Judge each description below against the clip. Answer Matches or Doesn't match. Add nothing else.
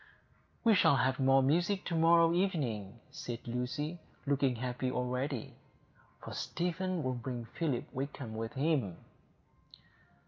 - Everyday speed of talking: Doesn't match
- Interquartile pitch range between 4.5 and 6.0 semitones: Matches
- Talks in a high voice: Doesn't match